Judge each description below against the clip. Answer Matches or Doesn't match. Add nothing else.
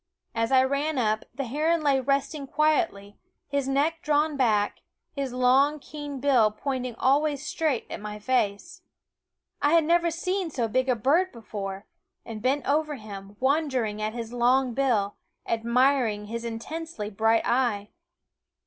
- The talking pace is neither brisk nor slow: Matches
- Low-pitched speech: Doesn't match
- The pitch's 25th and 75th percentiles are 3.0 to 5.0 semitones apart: Matches